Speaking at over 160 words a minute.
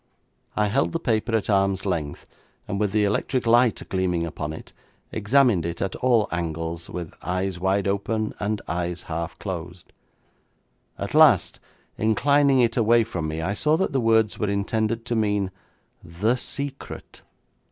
No: average, 155 wpm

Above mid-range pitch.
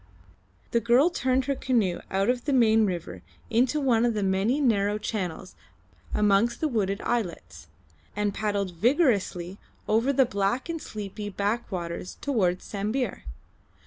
Yes: high, 215 Hz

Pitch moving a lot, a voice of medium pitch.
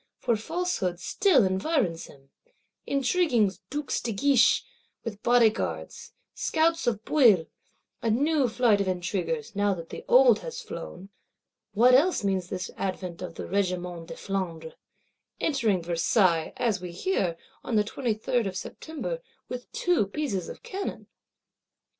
No: wide, 6.2 semitones; high, 215 Hz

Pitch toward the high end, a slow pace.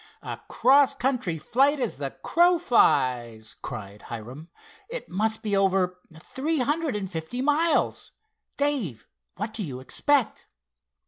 Yes: high, 215 Hz; slow, 130 wpm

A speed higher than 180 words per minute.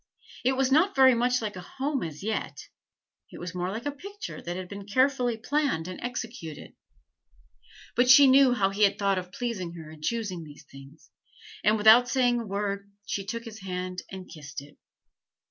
Yes: average, 190 wpm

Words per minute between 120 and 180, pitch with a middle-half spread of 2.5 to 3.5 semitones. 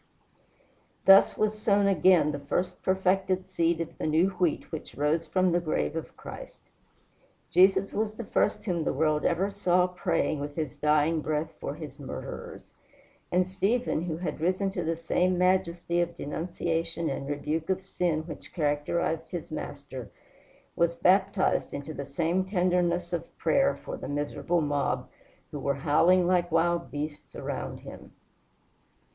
Yes: average, 155 wpm; average, 3.1 semitones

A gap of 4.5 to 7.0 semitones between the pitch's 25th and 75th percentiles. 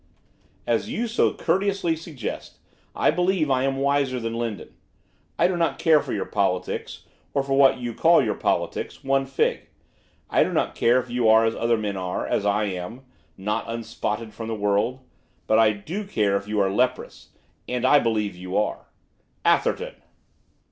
Yes: average, 4.8 semitones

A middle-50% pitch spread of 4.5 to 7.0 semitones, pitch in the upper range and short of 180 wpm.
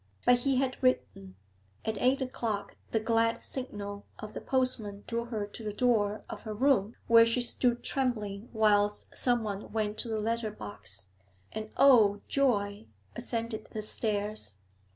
No: average, 2.9 semitones; high, 220 Hz; average, 150 wpm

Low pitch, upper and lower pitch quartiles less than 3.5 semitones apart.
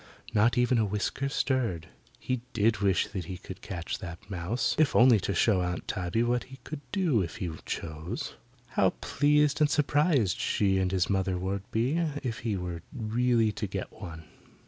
No: low, 105 Hz; average, 5.2 semitones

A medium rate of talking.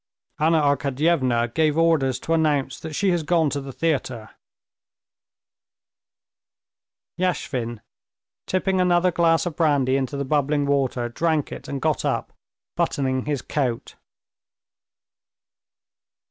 No: slow, 115 wpm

